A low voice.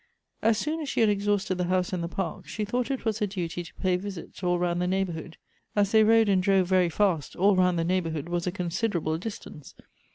No: medium, 185 Hz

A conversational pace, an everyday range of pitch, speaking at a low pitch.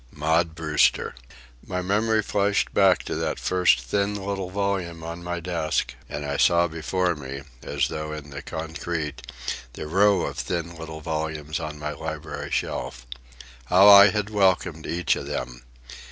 Yes: average, 155 wpm; average, 3.5 semitones; very low, 85 Hz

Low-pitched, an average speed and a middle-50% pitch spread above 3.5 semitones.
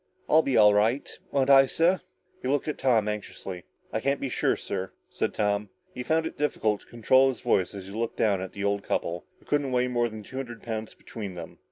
No: low, 115 Hz; fast, 230 wpm; average, 4.7 semitones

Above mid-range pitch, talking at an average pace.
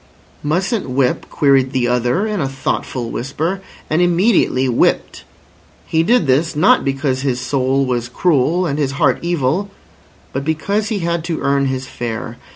No: medium, 140 Hz; average, 160 wpm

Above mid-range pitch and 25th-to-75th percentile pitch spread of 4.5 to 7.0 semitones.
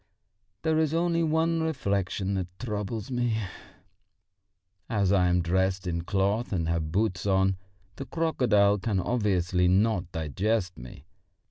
No: low, 100 Hz; average, 4.8 semitones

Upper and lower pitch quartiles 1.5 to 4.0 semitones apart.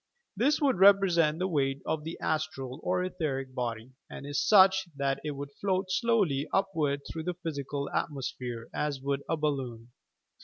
No: average, 5.2 semitones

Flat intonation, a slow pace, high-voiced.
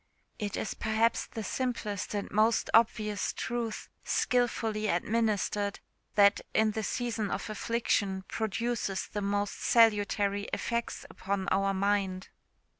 Yes: narrow, 2.2 semitones; slow, 115 wpm; high, 210 Hz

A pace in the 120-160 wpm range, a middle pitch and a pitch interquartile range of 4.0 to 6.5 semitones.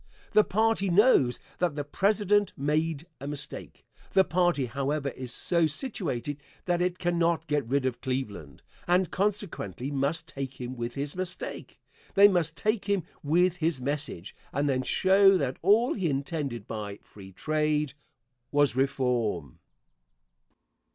Yes: average, 140 wpm; medium, 150 Hz; average, 5.3 semitones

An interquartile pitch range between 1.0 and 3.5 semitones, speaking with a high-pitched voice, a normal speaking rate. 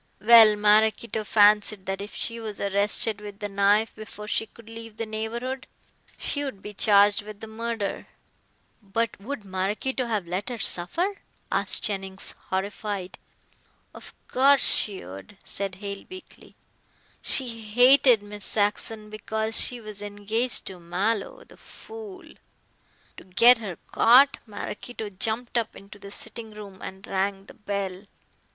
Yes: narrow, 2.4 semitones; high, 210 Hz; average, 145 wpm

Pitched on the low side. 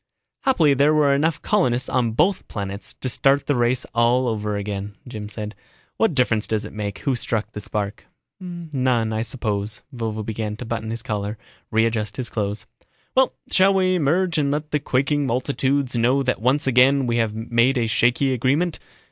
Yes: low, 120 Hz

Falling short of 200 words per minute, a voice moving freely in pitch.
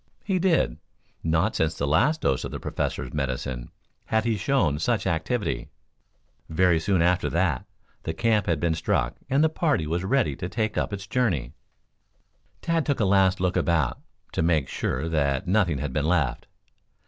Yes: average, 170 wpm; wide, 6.2 semitones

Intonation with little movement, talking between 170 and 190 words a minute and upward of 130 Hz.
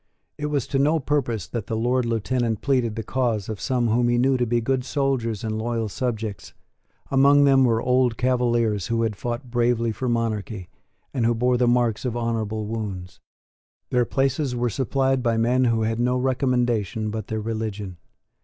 No: narrow, 2.3 semitones; average, 180 wpm; low, 120 Hz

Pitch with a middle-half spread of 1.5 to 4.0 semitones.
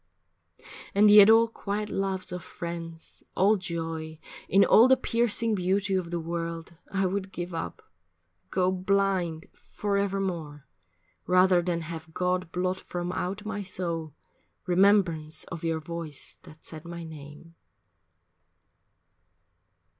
Yes: average, 2.9 semitones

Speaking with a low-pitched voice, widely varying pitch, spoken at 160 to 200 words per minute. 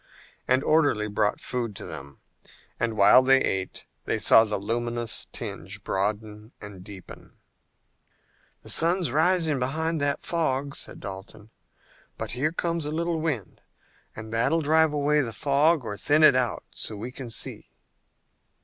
No: low, 130 Hz; wide, 6.3 semitones; average, 150 wpm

